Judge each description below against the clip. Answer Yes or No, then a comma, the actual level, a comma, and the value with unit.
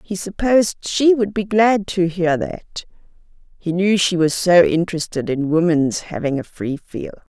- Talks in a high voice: No, medium, 180 Hz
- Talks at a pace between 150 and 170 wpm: Yes, average, 165 wpm